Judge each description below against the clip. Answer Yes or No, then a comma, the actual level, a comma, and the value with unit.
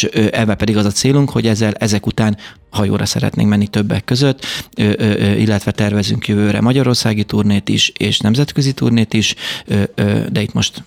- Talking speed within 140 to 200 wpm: Yes, average, 150 wpm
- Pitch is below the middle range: Yes, low, 110 Hz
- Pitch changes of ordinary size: No, narrow, 1.8 semitones